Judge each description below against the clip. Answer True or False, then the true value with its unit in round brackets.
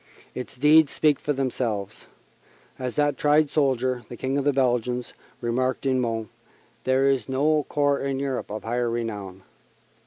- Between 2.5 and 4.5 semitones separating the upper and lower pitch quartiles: True (2.8 semitones)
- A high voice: False (130 Hz)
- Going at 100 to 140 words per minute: False (155 wpm)